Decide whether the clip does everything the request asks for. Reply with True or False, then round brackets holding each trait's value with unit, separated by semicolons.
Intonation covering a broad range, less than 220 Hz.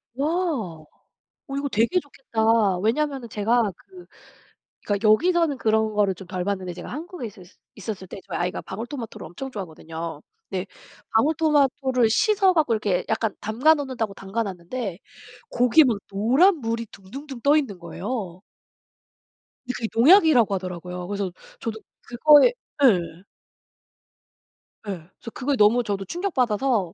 False (6.0 semitones; 225 Hz)